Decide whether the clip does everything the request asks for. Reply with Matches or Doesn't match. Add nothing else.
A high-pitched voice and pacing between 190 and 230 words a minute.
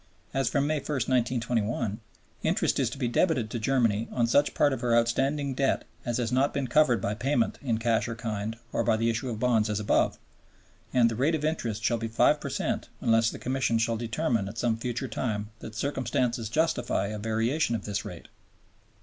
Doesn't match